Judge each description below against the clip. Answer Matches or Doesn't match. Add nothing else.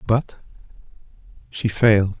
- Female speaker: Doesn't match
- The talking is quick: Doesn't match